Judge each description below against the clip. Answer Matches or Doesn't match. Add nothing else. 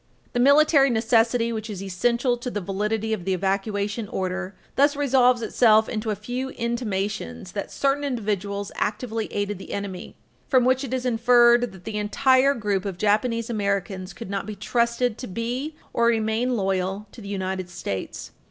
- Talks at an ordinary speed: Matches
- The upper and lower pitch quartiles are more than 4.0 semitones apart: Doesn't match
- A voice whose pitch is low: Doesn't match